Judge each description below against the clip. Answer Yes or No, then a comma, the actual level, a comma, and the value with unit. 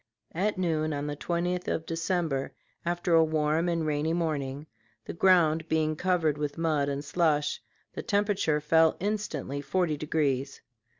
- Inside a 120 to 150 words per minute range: Yes, average, 145 wpm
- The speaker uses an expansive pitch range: No, average, 2.7 semitones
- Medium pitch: Yes, medium, 160 Hz